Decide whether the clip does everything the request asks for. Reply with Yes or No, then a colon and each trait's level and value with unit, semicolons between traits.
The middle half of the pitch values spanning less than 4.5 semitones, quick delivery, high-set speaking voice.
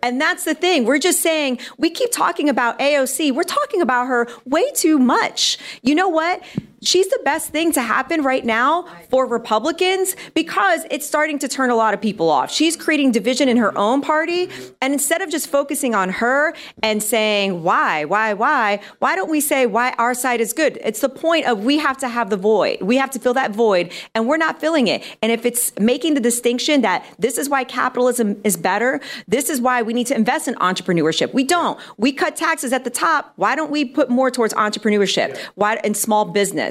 No: average, 5.1 semitones; fast, 215 wpm; very high, 260 Hz